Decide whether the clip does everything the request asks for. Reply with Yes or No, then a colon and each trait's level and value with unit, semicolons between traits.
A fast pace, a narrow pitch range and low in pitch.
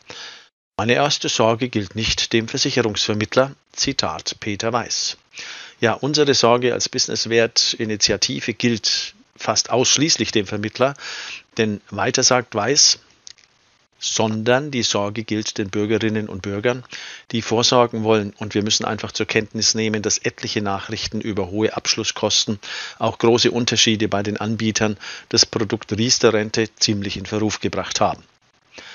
No: average, 135 wpm; narrow, 2.1 semitones; low, 110 Hz